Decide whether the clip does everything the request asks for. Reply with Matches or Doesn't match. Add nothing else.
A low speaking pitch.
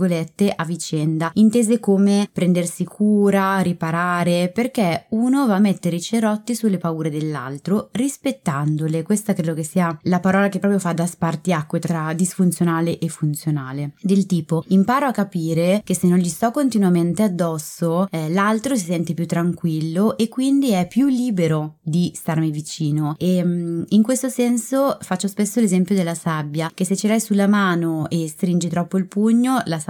Doesn't match